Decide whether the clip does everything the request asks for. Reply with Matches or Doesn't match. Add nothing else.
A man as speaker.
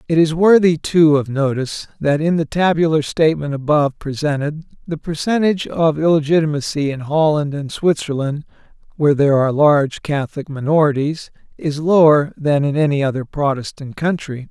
Matches